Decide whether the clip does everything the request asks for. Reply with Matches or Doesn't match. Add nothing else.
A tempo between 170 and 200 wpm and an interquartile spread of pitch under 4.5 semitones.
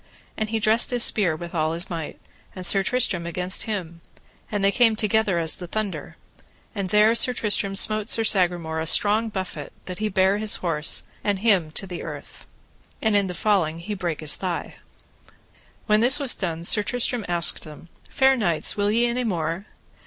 Matches